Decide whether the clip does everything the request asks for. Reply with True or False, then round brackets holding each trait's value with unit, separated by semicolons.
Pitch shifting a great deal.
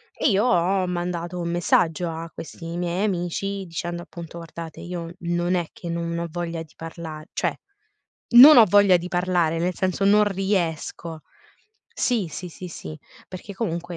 False (1.8 semitones)